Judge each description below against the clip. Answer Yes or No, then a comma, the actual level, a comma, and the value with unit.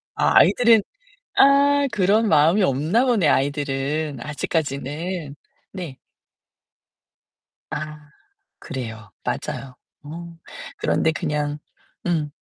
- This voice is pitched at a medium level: Yes, medium, 155 Hz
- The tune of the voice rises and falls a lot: No, average, 4.6 semitones